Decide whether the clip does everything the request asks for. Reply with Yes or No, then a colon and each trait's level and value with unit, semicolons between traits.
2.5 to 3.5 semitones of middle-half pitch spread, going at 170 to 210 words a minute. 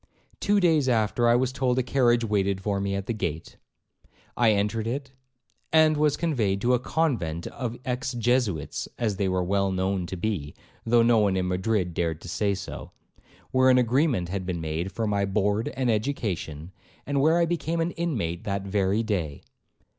No: average, 5.2 semitones; average, 185 wpm